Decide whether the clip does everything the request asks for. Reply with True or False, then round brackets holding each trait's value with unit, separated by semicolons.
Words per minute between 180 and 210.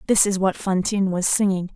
True (205 wpm)